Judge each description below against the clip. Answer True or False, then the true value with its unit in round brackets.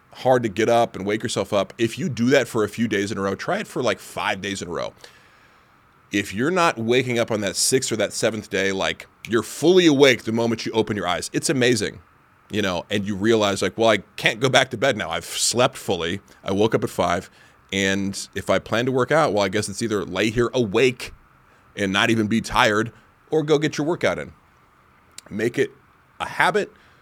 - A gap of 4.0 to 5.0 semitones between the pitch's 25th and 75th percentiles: False (3.4 semitones)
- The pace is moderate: False (230 wpm)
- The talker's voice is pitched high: False (110 Hz)